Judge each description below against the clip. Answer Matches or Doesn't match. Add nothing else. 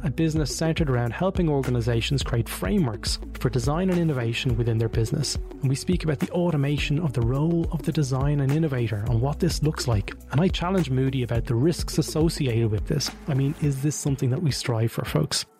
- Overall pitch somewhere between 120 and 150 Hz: Matches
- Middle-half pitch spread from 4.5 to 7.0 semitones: Matches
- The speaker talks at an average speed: Doesn't match